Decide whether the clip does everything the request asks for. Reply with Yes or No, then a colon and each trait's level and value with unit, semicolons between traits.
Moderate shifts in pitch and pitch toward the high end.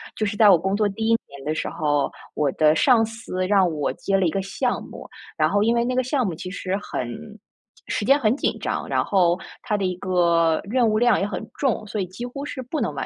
Yes: average, 4.5 semitones; high, 200 Hz